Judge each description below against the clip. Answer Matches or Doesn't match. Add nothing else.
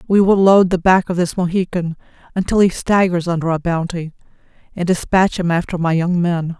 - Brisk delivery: Doesn't match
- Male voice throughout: Doesn't match